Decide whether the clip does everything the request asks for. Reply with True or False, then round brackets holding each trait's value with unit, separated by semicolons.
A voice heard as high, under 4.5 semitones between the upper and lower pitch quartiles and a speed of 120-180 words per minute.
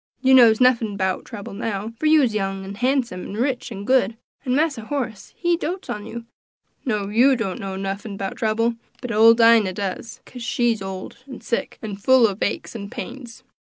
False (225 Hz; 3.9 semitones; 190 wpm)